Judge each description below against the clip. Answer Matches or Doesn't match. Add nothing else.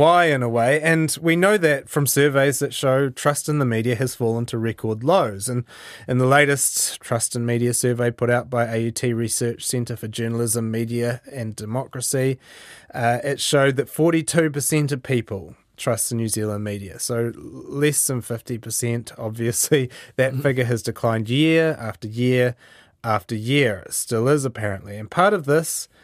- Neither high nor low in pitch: Doesn't match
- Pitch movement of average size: Matches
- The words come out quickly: Doesn't match